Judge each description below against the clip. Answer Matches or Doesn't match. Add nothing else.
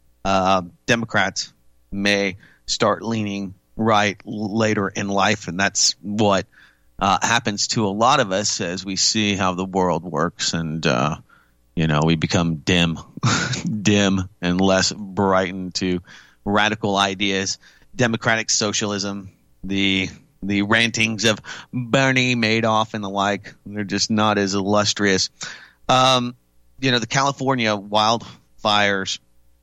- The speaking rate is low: Matches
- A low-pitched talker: Matches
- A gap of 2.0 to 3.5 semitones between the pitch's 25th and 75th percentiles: Matches